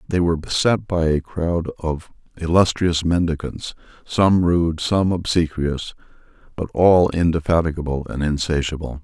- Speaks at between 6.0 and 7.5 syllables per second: No, 4.5 syllables/s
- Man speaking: Yes, male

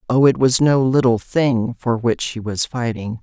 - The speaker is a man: No, female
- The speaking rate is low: No, fast, 205 wpm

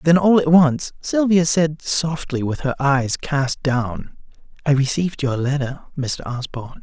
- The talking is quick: No, average, 160 wpm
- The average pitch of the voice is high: No, medium, 145 Hz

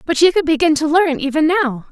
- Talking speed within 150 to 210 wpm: No, fast, 250 wpm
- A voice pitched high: Yes, very high, 310 Hz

